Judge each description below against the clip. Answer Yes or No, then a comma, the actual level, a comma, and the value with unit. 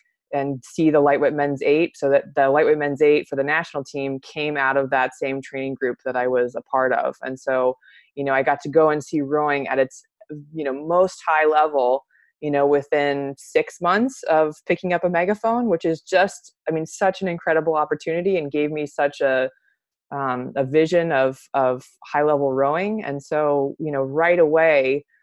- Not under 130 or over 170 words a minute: No, average, 200 wpm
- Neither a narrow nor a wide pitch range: Yes, average, 3.0 semitones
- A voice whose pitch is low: No, medium, 150 Hz